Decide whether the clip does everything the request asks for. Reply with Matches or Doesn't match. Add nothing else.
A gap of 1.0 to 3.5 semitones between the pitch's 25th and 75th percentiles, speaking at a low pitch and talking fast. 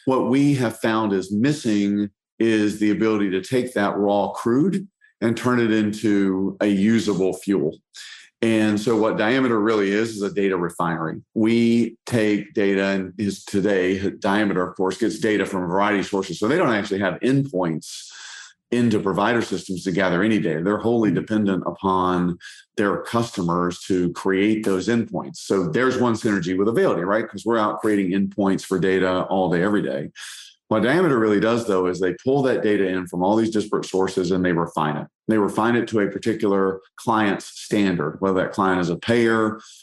Doesn't match